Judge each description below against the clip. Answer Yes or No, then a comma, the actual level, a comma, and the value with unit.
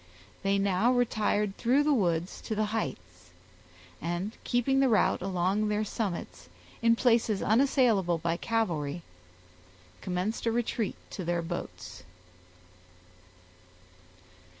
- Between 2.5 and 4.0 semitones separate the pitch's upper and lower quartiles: No, average, 4.8 semitones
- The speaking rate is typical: No, slow, 110 wpm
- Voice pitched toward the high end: Yes, high, 210 Hz